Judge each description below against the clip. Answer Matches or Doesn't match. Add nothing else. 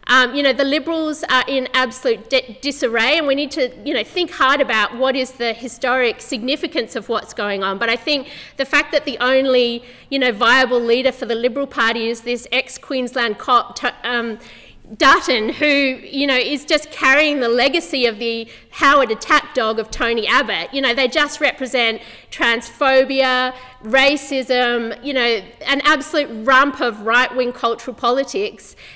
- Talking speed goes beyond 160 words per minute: Matches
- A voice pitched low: Doesn't match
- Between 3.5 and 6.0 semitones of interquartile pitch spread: Doesn't match